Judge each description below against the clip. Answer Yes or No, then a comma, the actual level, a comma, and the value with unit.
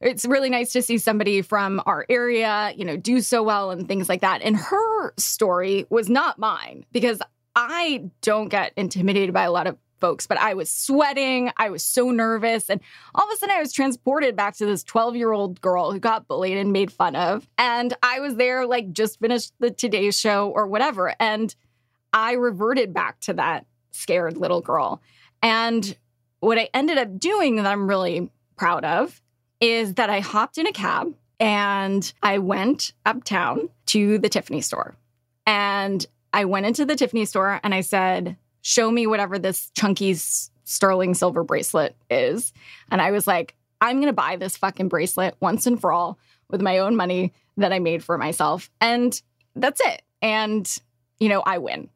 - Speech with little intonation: No, average, 4.1 semitones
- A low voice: No, high, 210 Hz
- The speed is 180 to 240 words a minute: Yes, average, 185 wpm